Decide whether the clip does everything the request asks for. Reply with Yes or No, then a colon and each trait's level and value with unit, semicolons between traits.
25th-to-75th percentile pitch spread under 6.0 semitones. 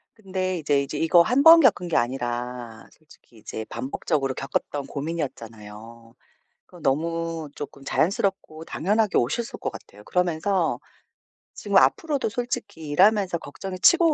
No: wide, 6.3 semitones